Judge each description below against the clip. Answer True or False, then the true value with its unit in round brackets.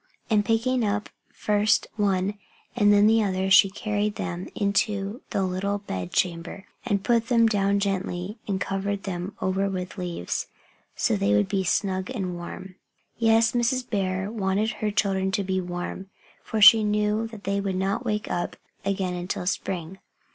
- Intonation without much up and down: True (2.1 semitones)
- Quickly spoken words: False (165 wpm)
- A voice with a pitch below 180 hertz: False (200 Hz)